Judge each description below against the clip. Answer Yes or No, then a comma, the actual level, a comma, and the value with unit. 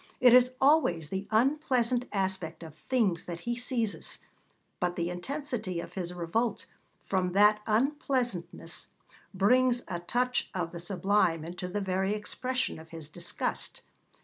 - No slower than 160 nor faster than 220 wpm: No, average, 140 wpm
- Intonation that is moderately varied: No, wide, 5.9 semitones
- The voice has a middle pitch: No, high, 200 Hz